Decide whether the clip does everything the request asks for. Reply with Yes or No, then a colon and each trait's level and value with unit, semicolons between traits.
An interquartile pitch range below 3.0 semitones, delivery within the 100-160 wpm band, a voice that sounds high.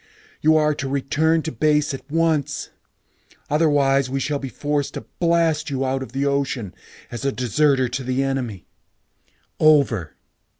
No: narrow, 2.4 semitones; average, 155 wpm; medium, 140 Hz